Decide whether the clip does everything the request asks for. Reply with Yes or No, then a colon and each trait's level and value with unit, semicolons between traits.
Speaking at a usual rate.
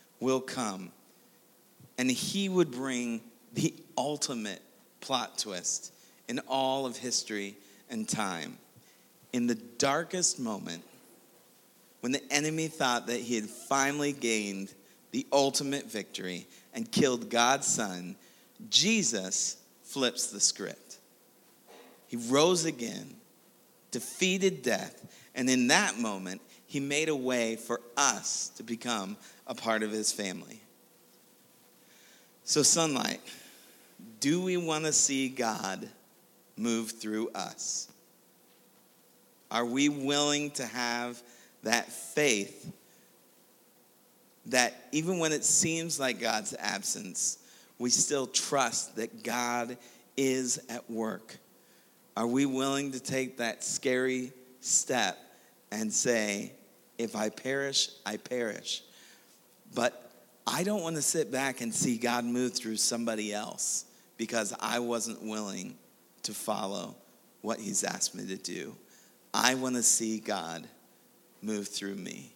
No: slow, 120 wpm